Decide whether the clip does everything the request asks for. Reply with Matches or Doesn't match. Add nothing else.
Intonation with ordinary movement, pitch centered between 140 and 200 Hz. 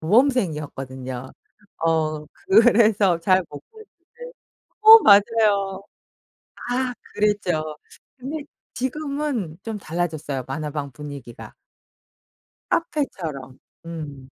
Doesn't match